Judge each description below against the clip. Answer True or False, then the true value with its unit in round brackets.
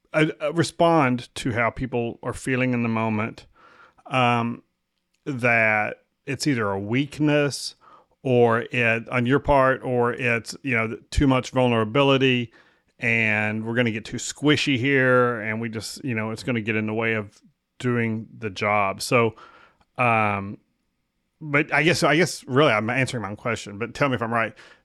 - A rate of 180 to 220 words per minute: False (170 wpm)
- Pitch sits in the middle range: False (120 Hz)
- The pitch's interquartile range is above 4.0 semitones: False (3.0 semitones)